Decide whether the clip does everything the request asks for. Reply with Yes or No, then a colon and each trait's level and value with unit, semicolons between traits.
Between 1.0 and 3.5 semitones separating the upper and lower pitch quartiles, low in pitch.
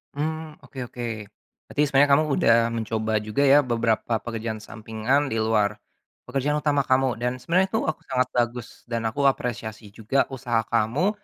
No: average, 4.0 semitones; low, 120 Hz